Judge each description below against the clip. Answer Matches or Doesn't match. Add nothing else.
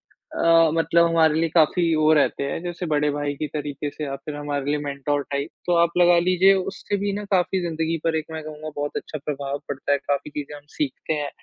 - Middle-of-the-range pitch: Matches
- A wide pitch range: Doesn't match